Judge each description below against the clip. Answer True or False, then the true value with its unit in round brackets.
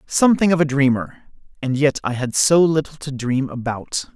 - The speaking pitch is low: False (145 Hz)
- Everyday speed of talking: True (190 wpm)